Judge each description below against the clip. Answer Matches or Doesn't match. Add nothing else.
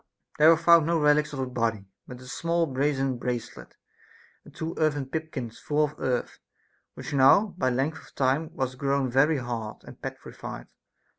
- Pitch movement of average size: Matches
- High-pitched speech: Doesn't match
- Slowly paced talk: Doesn't match